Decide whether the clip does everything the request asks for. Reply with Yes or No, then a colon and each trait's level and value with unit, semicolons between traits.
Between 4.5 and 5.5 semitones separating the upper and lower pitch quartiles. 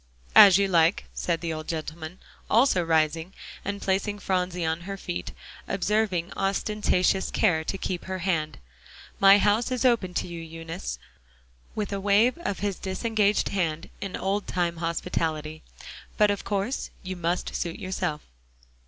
No: average, 3.3 semitones